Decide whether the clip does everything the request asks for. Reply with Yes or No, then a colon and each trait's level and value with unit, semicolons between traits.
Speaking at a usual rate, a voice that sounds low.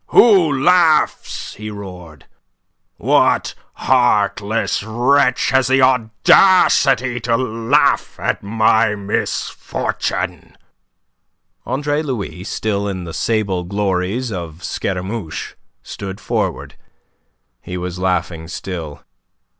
No: slow, 90 wpm; low, 110 Hz